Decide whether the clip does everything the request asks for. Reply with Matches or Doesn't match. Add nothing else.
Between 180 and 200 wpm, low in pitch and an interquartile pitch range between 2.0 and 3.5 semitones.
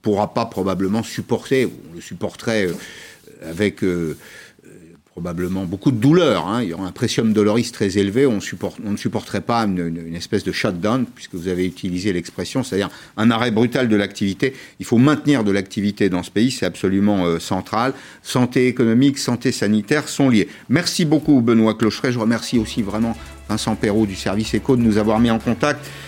Doesn't match